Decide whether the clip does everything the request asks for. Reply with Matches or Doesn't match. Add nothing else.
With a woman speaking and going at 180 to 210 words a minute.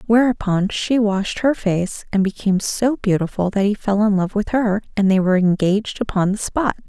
Matches